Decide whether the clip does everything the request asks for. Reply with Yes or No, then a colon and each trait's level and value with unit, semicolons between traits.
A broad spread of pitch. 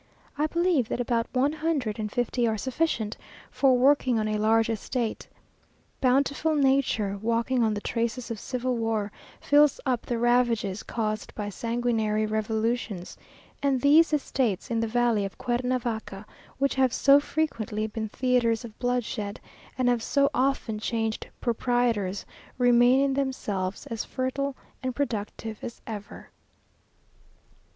No: average, 3.2 semitones